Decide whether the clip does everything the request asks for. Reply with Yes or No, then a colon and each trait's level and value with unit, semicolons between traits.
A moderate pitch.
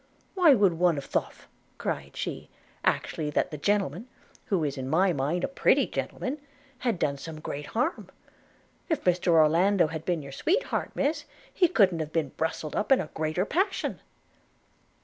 Yes: medium, 175 Hz